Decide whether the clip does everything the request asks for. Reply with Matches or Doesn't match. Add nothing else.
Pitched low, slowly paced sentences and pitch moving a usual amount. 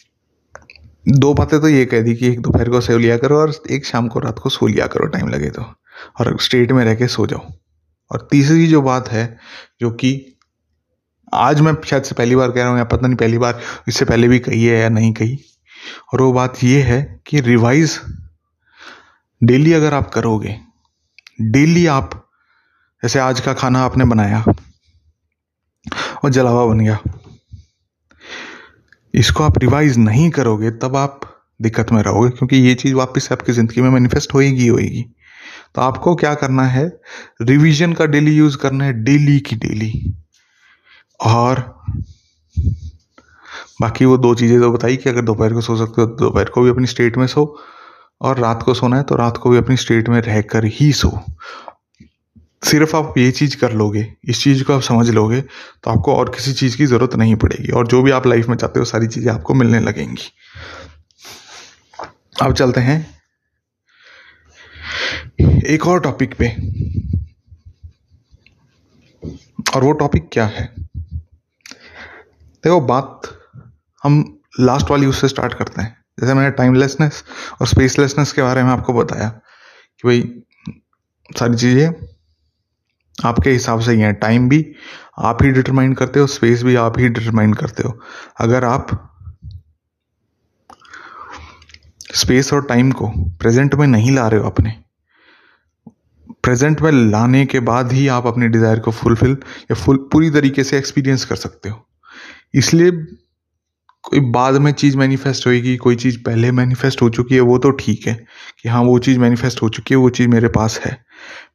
Doesn't match